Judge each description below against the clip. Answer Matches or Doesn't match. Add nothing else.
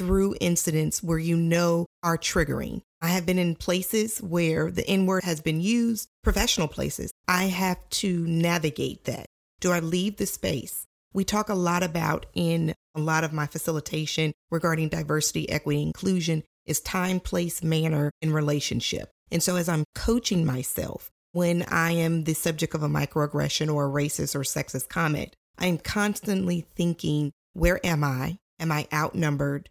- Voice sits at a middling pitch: Matches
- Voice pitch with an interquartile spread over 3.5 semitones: Doesn't match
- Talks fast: Doesn't match